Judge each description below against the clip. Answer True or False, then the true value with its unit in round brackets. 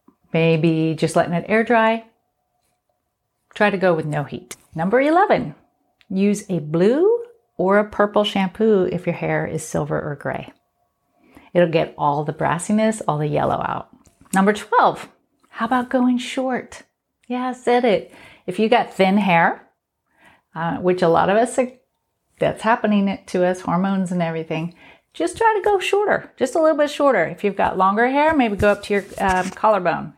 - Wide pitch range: True (6.4 semitones)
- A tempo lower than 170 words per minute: False (175 wpm)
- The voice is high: True (205 Hz)